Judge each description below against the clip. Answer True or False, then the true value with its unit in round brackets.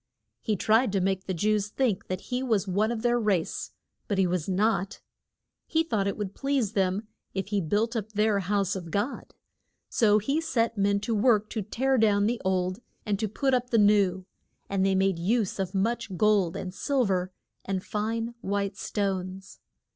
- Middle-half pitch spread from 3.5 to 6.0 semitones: False (2.9 semitones)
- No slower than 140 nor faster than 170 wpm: False (190 wpm)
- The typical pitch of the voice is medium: False (205 Hz)